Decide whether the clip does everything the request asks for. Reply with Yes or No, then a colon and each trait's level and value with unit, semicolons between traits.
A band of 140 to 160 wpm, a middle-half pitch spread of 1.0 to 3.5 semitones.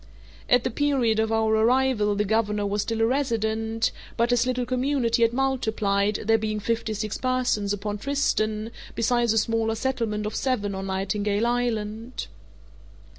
Yes: average, 155 wpm; narrow, 2.5 semitones